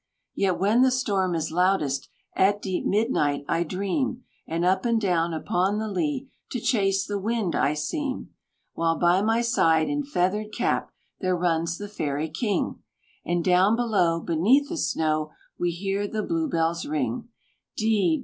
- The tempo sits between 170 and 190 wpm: No, average, 160 wpm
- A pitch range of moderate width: Yes, average, 4.8 semitones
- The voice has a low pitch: No, high, 190 Hz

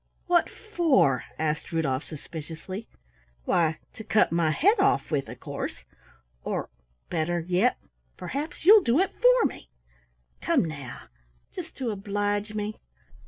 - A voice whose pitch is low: No, high, 205 Hz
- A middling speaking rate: No, slow, 130 wpm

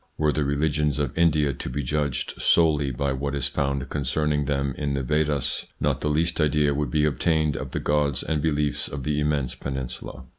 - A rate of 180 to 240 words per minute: Yes, average, 200 wpm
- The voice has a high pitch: No, very low, 75 Hz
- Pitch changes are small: Yes, narrow, 1.5 semitones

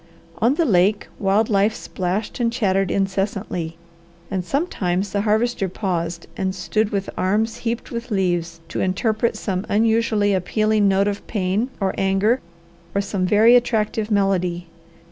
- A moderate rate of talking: Yes, average, 145 wpm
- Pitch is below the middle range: No, high, 200 Hz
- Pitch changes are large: No, average, 2.8 semitones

